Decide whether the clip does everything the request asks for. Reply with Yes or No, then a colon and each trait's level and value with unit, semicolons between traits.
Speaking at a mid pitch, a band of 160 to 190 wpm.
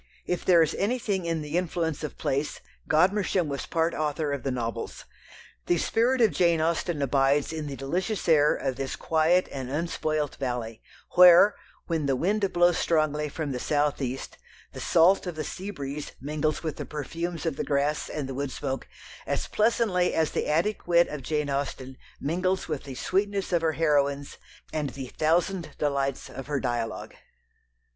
Yes: medium, 155 Hz; average, 175 wpm